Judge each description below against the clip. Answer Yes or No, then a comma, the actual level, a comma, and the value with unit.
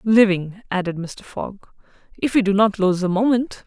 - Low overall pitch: No, high, 200 Hz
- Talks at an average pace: Yes, average, 180 wpm